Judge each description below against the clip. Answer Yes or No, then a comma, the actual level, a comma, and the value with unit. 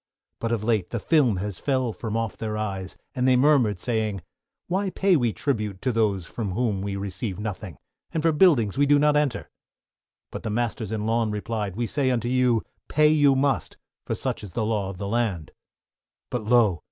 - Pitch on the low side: Yes, low, 115 Hz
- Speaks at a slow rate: No, average, 200 wpm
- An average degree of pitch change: Yes, average, 4.0 semitones